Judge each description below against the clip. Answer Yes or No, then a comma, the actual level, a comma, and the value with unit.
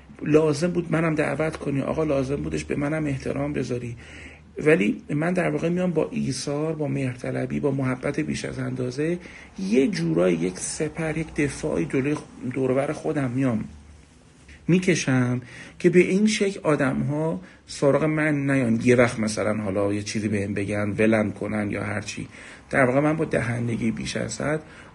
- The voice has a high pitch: No, medium, 140 Hz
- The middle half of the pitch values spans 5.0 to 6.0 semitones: Yes, wide, 5.6 semitones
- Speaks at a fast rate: Yes, fast, 160 wpm